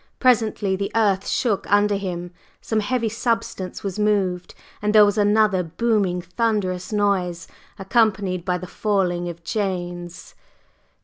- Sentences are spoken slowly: Yes, slow, 130 wpm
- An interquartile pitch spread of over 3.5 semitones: No, average, 3.0 semitones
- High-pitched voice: Yes, high, 200 Hz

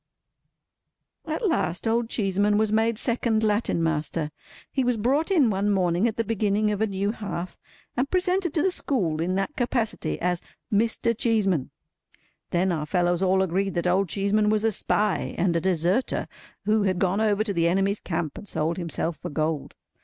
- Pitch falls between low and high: No, high, 200 Hz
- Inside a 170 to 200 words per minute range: Yes, average, 180 wpm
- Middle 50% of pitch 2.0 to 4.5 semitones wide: Yes, average, 4.1 semitones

